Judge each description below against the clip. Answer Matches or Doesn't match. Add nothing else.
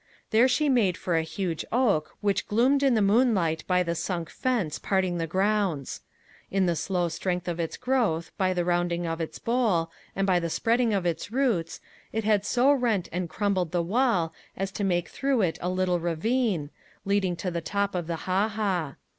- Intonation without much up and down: Doesn't match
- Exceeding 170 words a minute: Matches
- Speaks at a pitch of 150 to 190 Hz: Matches